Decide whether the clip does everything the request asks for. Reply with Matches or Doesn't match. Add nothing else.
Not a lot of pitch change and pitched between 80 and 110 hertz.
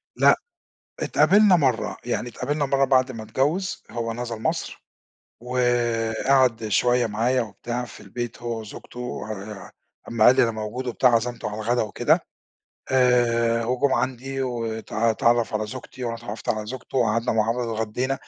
Doesn't match